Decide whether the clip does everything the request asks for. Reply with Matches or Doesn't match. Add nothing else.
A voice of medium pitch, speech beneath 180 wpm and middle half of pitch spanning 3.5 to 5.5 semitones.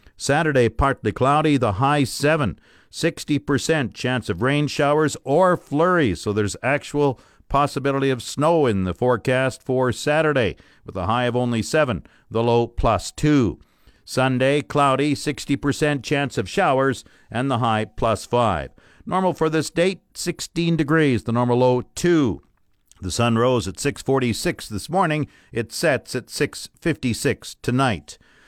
Doesn't match